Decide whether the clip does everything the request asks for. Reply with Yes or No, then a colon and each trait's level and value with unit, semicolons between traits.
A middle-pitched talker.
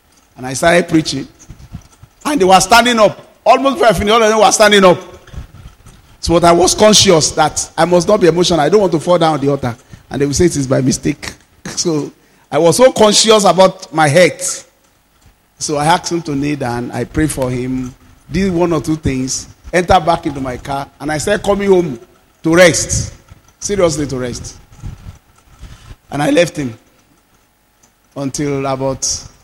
Yes: medium, 155 Hz